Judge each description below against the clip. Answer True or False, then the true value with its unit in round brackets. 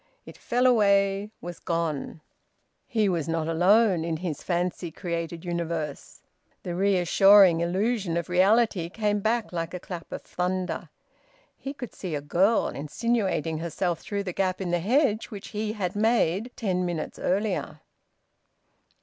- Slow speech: False (145 wpm)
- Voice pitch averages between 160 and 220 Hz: True (185 Hz)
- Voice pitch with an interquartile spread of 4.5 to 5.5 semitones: False (3.6 semitones)